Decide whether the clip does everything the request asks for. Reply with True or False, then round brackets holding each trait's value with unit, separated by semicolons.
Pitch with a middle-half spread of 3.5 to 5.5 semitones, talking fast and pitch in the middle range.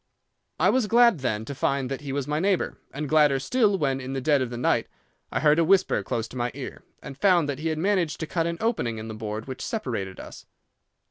True (5.2 semitones; 245 wpm; 145 Hz)